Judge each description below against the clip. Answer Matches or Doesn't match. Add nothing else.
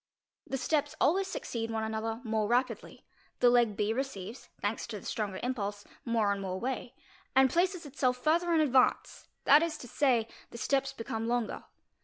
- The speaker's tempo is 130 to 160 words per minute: Doesn't match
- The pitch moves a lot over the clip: Doesn't match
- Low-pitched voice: Doesn't match